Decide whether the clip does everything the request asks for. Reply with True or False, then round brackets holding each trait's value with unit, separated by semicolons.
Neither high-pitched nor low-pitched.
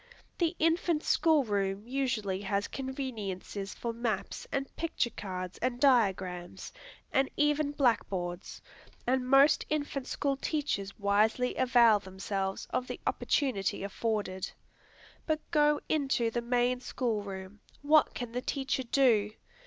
False (240 Hz)